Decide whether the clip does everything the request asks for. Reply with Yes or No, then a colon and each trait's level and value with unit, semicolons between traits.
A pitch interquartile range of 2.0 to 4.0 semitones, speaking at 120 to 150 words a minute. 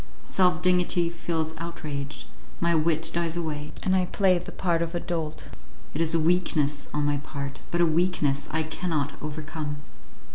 No: narrow, 2.5 semitones; average, 170 wpm